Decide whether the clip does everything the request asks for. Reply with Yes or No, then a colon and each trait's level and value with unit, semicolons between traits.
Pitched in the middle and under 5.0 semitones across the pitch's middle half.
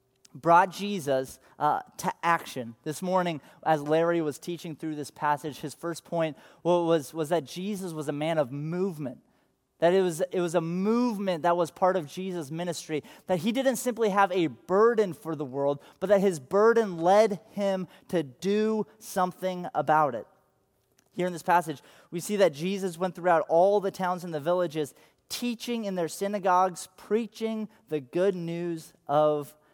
Yes: medium, 175 Hz; average, 3.9 semitones